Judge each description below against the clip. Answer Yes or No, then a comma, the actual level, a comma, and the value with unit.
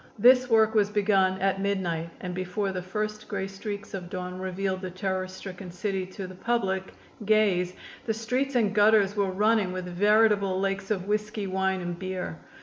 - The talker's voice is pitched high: Yes, high, 195 Hz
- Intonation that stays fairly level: Yes, narrow, 2.2 semitones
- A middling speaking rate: Yes, average, 175 wpm